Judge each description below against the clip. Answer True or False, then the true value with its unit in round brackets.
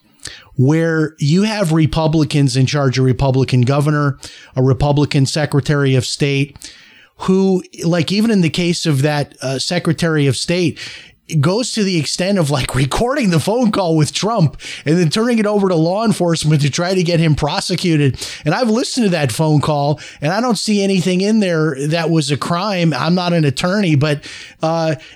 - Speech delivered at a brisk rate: False (180 wpm)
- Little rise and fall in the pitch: False (4.0 semitones)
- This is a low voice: False (160 Hz)